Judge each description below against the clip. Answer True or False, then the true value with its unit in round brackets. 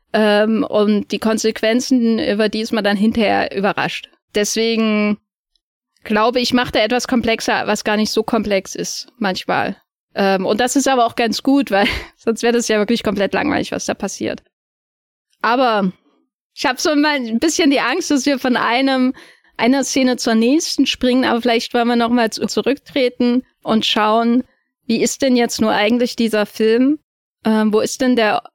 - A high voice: True (230 Hz)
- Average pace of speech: True (170 wpm)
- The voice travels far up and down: False (2.8 semitones)